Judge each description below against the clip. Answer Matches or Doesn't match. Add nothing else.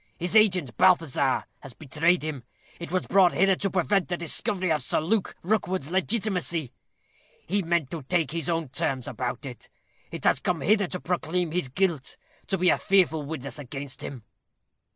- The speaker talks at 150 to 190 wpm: Matches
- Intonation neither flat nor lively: Matches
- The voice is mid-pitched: Matches